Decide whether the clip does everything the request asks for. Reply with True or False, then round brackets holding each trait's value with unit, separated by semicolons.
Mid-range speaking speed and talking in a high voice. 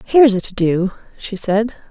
True (190 wpm; 205 Hz)